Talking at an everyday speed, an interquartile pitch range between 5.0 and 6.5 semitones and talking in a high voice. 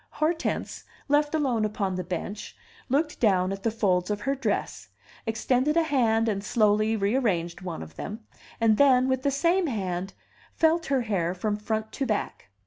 Yes: average, 170 wpm; wide, 5.5 semitones; high, 220 Hz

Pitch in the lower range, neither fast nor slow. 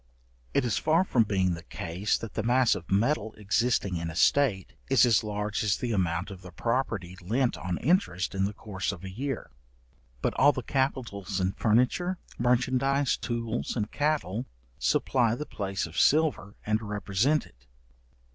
Yes: low, 110 Hz; average, 170 wpm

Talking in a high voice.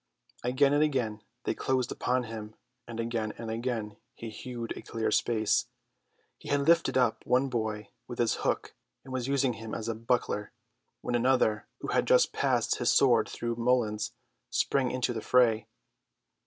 No: low, 120 Hz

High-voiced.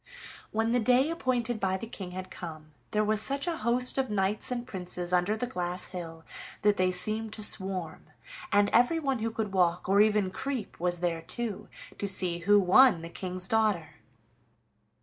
Yes: high, 205 Hz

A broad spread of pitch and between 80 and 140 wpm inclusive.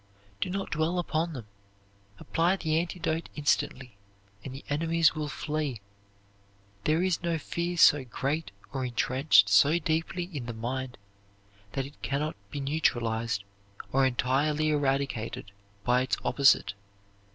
No: average, 4.0 semitones; slow, 135 wpm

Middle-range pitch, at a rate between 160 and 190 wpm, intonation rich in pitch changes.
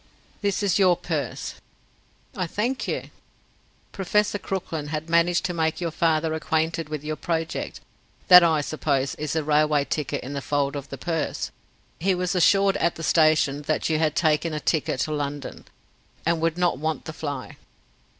No: medium, 160 Hz; average, 170 wpm; narrow, 2.4 semitones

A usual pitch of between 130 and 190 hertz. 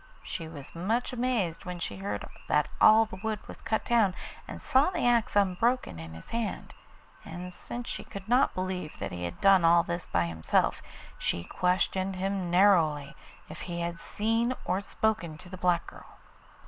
Yes: medium, 185 Hz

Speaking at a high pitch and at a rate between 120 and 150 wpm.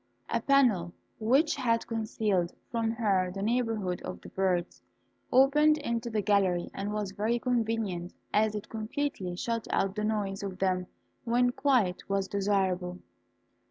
Yes: high, 210 Hz; average, 145 wpm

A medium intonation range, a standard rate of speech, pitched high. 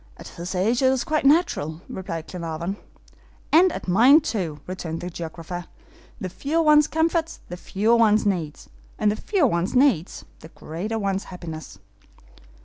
No: wide, 8.1 semitones; average, 155 wpm; high, 195 Hz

